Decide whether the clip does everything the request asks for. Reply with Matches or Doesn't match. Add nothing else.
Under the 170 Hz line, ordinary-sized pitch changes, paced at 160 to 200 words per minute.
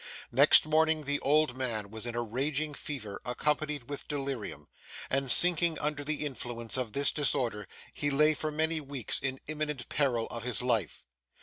Matches